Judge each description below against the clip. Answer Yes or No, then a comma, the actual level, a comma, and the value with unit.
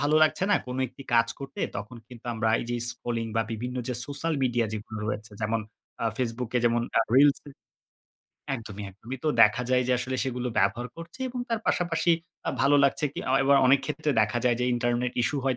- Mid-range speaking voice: No, low, 125 Hz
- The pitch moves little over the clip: No, average, 3.2 semitones